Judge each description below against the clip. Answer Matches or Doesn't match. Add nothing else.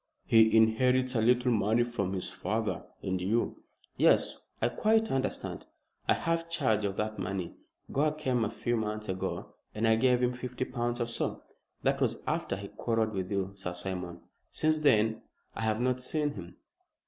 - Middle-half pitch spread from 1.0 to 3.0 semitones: Doesn't match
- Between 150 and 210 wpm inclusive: Matches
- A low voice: Matches